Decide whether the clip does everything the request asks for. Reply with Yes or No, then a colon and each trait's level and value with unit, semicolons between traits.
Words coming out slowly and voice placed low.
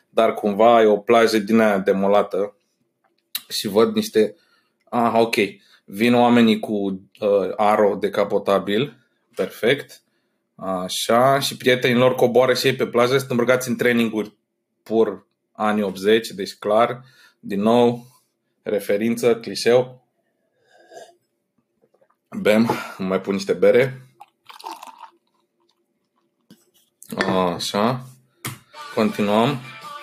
Yes: slow, 100 wpm; low, 115 Hz